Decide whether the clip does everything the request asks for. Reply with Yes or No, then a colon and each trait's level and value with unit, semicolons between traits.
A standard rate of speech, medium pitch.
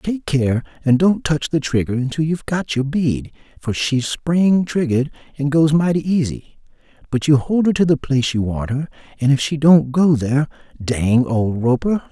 Yes: average, 195 wpm; medium, 145 Hz